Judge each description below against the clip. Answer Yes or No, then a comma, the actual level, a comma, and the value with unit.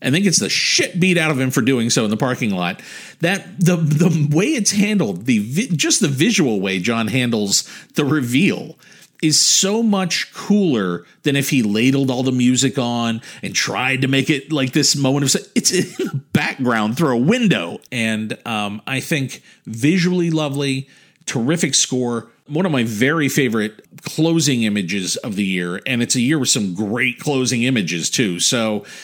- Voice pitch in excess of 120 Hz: Yes, low, 135 Hz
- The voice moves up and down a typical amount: No, wide, 5.9 semitones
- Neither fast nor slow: Yes, average, 185 wpm